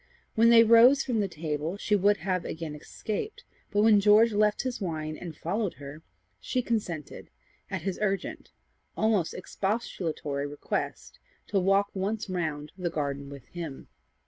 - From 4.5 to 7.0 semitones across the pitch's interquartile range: Yes, average, 5.3 semitones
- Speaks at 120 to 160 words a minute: Yes, average, 150 wpm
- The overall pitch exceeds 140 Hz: Yes, high, 190 Hz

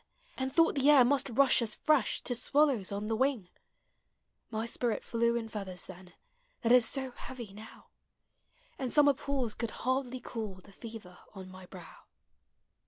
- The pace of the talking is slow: No, average, 165 wpm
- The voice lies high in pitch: Yes, high, 235 Hz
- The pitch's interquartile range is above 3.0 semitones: Yes, average, 4.0 semitones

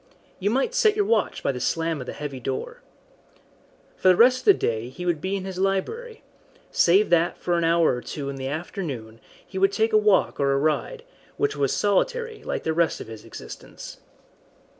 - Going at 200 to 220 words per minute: Yes, fast, 205 wpm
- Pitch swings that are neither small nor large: No, wide, 7.9 semitones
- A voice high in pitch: No, medium, 180 Hz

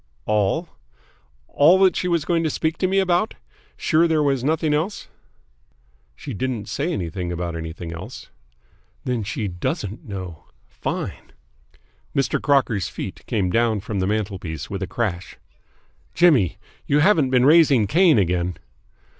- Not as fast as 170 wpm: Yes, average, 140 wpm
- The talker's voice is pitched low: Yes, low, 120 Hz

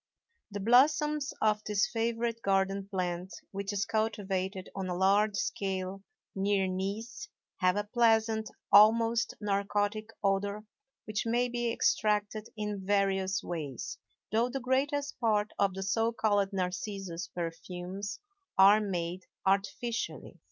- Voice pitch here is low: No, high, 205 Hz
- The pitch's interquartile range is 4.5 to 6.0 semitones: No, average, 2.7 semitones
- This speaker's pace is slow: Yes, slow, 125 wpm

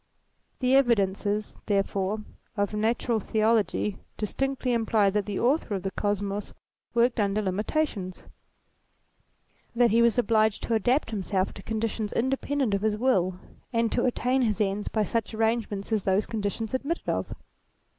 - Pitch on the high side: Yes, high, 215 Hz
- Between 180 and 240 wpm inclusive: No, average, 145 wpm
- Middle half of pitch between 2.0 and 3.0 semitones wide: Yes, average, 2.7 semitones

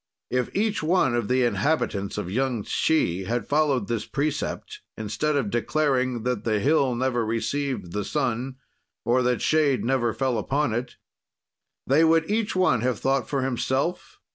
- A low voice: Yes, low, 130 Hz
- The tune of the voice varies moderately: Yes, average, 3.9 semitones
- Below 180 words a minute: Yes, average, 160 wpm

